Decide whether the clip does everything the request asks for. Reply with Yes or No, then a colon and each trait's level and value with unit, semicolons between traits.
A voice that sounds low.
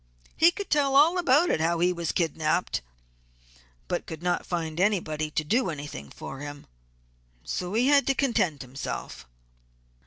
No: medium, 175 Hz